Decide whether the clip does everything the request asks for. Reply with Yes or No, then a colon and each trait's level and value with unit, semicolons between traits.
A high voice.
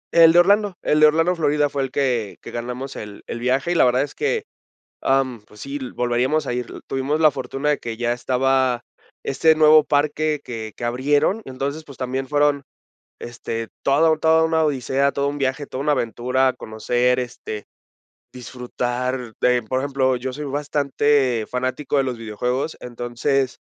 No: low, 135 Hz